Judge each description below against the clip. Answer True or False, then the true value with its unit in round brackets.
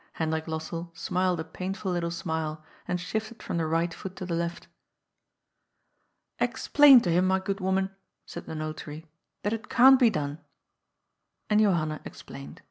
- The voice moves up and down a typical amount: True (3.2 semitones)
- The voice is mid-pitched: True (175 Hz)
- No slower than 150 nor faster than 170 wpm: True (160 wpm)